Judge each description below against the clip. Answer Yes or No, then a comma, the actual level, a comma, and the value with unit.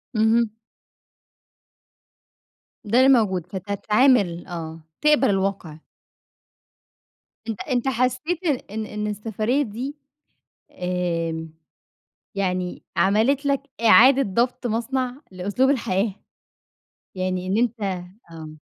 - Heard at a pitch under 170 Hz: No, high, 215 Hz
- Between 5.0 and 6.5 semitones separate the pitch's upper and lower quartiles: Yes, wide, 5.5 semitones